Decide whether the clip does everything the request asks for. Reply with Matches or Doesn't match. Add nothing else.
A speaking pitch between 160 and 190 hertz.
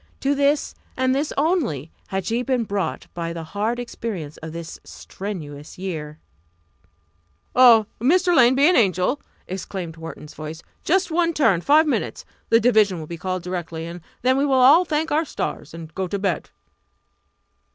Doesn't match